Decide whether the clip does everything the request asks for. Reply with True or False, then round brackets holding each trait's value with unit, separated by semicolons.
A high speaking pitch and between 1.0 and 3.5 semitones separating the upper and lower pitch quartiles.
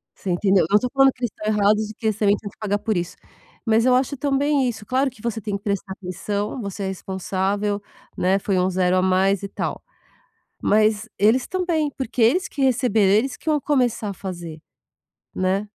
False (210 Hz; 4.5 semitones)